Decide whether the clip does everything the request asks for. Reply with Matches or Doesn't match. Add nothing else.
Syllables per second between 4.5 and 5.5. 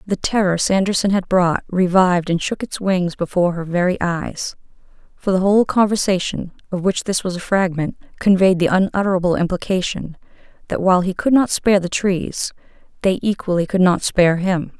Matches